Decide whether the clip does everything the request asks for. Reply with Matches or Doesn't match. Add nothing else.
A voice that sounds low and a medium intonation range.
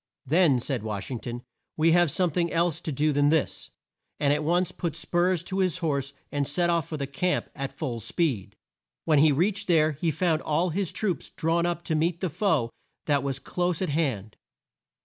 Doesn't match